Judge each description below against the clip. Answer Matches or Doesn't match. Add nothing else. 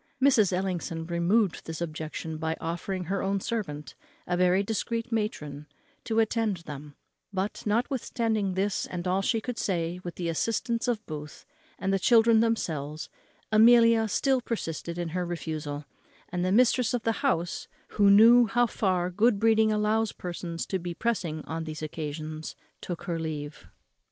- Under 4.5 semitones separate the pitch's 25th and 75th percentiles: Doesn't match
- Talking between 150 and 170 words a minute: Matches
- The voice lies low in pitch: Doesn't match